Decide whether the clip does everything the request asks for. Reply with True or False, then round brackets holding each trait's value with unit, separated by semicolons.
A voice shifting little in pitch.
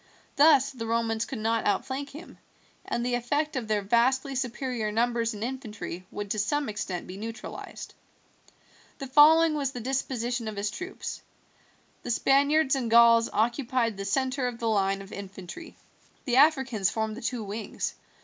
False (3.7 semitones)